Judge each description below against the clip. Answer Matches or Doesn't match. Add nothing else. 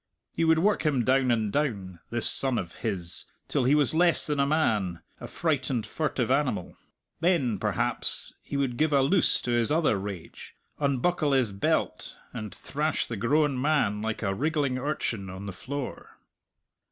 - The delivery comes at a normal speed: Matches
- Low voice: Matches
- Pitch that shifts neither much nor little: Doesn't match